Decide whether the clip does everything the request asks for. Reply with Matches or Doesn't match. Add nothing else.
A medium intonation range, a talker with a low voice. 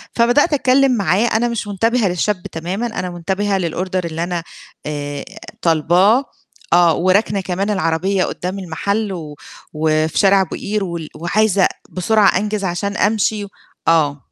Doesn't match